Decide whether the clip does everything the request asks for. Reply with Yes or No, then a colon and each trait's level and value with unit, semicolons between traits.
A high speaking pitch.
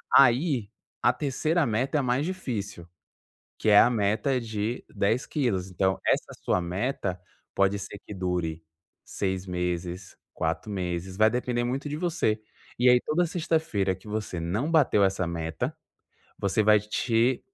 No: low, 105 Hz